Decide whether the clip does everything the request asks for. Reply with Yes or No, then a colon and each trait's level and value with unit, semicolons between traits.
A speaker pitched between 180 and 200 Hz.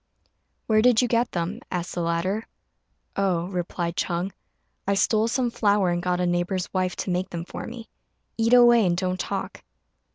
Yes: medium, 185 Hz